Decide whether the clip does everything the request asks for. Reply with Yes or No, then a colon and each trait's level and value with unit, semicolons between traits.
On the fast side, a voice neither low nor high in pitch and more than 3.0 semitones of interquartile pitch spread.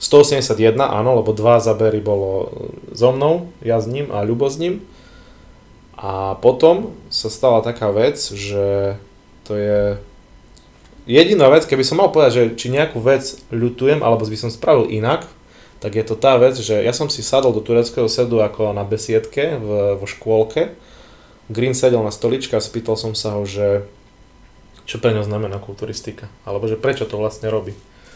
No: fast, 170 wpm; low, 110 Hz; average, 3.7 semitones